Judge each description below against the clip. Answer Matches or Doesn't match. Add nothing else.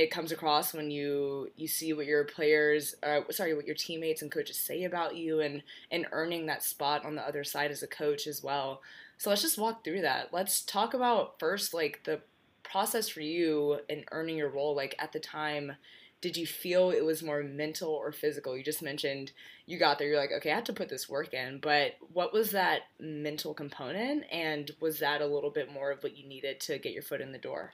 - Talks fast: Matches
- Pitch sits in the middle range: Matches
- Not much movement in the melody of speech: Matches